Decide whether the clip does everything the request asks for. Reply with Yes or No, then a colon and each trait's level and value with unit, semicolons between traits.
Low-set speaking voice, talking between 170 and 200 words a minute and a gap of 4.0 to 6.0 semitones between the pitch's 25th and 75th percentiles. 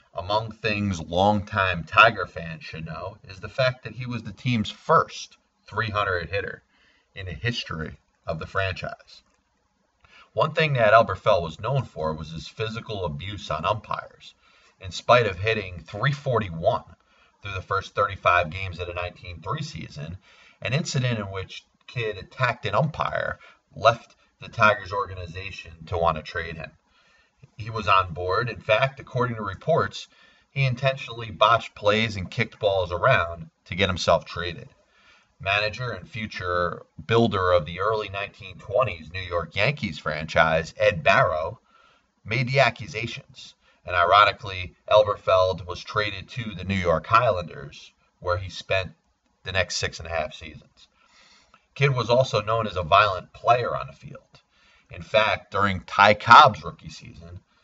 No: low, 100 Hz; average, 150 wpm; average, 4.3 semitones